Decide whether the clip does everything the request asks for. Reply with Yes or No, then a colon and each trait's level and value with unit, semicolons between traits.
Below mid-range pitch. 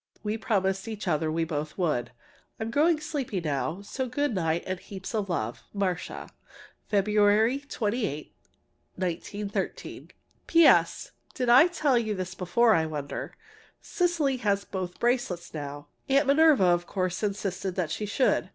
No: high, 200 Hz